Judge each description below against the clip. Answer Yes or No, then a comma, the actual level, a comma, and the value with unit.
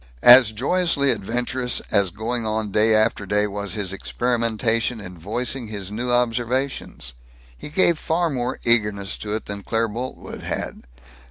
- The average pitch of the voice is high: No, low, 115 Hz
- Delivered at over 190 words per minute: No, average, 150 wpm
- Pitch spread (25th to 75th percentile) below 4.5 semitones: Yes, average, 3.0 semitones